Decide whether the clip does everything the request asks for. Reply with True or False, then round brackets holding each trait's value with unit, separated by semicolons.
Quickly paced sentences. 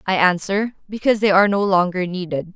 False (190 wpm)